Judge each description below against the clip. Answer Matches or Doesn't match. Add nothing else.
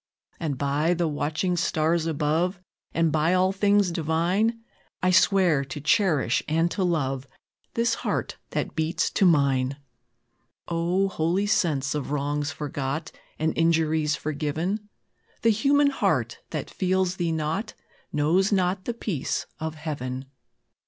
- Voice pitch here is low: Doesn't match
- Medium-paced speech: Doesn't match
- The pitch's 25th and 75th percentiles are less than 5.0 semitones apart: Matches